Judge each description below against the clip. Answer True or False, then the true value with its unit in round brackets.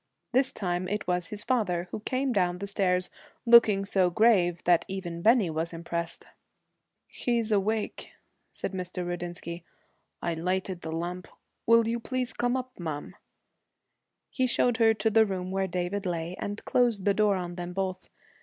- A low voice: False (190 Hz)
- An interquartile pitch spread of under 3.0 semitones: False (4.0 semitones)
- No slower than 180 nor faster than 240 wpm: False (165 wpm)